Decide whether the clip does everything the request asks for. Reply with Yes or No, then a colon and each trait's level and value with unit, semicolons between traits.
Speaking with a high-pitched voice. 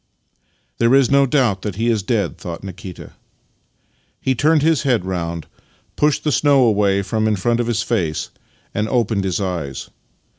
No: low, 110 Hz